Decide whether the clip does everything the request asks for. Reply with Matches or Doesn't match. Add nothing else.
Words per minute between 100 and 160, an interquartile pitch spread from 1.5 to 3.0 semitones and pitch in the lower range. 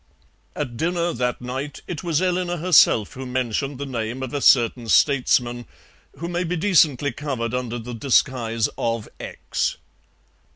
Doesn't match